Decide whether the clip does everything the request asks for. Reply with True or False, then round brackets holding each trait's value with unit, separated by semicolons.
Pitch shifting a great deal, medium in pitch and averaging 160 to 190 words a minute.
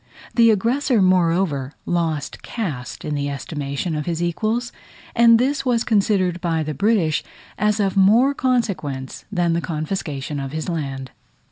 False (6.4 semitones; 175 Hz; 145 wpm)